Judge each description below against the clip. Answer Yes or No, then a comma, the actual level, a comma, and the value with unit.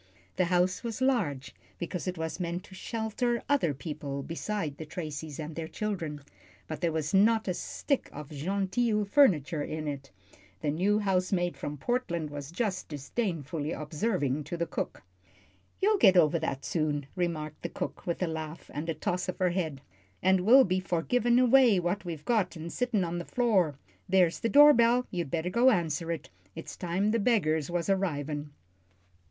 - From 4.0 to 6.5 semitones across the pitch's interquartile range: Yes, average, 5.1 semitones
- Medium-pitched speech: Yes, medium, 175 Hz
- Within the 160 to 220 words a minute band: Yes, average, 180 wpm